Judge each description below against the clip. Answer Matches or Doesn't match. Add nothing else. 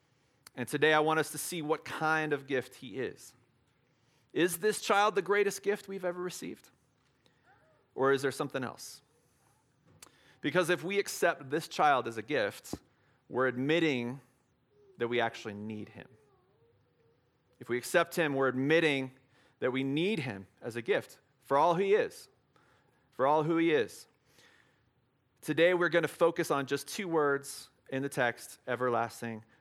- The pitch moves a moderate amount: Matches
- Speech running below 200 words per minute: Matches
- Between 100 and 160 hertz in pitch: Matches